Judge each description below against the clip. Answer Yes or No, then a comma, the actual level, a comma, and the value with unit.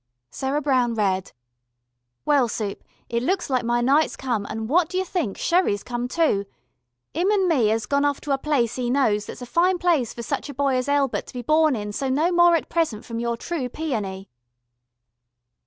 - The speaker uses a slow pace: No, average, 200 wpm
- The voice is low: No, very high, 265 Hz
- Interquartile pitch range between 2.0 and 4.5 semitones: No, average, 5.2 semitones